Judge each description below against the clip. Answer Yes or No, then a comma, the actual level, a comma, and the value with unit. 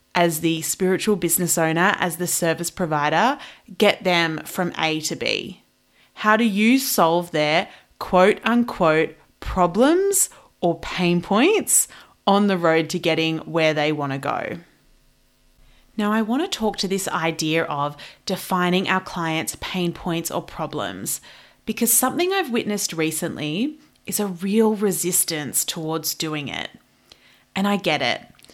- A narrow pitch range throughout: No, average, 4.4 semitones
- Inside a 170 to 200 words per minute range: No, average, 145 wpm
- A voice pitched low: No, medium, 180 Hz